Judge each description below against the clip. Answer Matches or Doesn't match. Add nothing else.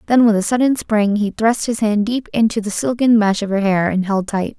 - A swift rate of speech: Matches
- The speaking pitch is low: Doesn't match